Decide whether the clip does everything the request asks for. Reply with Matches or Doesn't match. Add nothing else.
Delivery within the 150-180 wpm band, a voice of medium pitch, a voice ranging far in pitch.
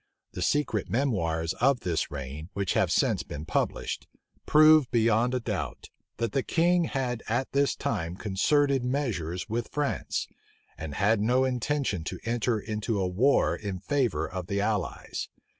Doesn't match